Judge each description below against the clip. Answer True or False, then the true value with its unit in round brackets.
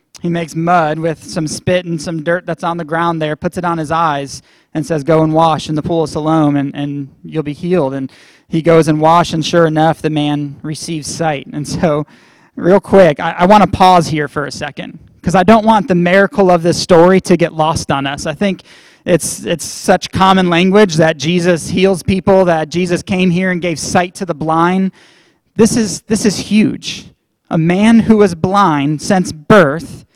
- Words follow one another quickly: True (210 wpm)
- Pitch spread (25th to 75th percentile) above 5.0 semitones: False (2.9 semitones)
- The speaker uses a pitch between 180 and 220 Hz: False (170 Hz)